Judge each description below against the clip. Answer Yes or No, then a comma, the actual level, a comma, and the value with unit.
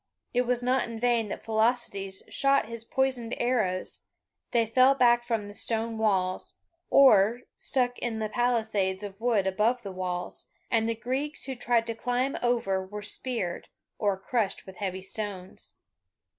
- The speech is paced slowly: No, average, 155 wpm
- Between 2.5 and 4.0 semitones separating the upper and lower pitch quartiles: Yes, average, 3.5 semitones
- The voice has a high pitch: Yes, high, 225 Hz